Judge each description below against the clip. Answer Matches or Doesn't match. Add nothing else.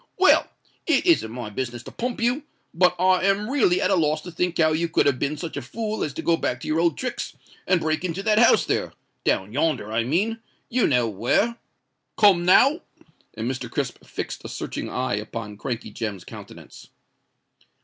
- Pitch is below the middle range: Doesn't match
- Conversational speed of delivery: Matches